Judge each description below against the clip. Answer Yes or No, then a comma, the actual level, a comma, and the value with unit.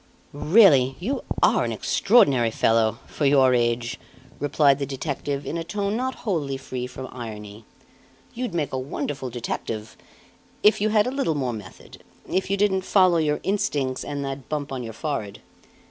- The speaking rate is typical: Yes, average, 165 wpm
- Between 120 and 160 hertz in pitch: Yes, medium, 140 Hz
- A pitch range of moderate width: No, wide, 6.7 semitones